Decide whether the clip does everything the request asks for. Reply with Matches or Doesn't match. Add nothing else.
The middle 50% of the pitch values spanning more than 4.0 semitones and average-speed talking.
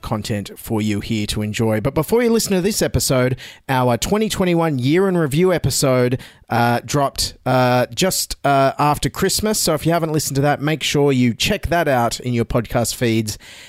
Matches